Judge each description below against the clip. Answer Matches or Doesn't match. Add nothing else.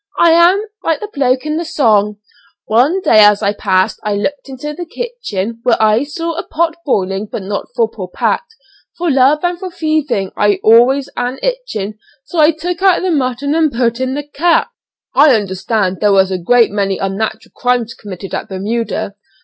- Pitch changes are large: Matches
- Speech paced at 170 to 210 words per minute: Matches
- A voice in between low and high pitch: Doesn't match